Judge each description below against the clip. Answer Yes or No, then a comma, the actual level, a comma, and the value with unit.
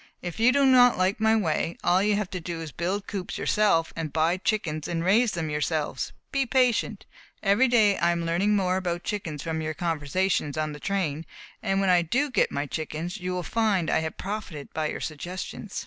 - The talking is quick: Yes, fast, 210 wpm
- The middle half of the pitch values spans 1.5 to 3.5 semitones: No, average, 4.5 semitones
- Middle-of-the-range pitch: Yes, medium, 180 Hz